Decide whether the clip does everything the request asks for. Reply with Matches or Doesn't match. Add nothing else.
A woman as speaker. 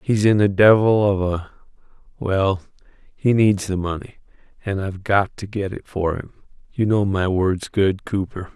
Doesn't match